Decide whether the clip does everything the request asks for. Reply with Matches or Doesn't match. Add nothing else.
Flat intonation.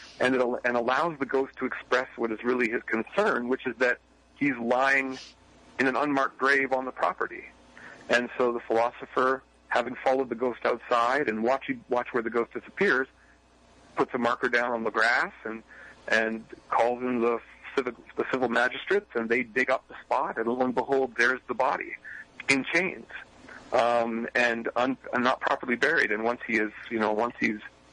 Matches